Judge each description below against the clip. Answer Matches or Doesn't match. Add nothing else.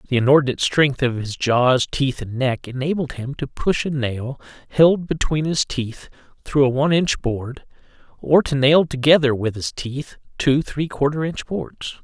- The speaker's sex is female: Doesn't match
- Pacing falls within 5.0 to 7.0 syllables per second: Doesn't match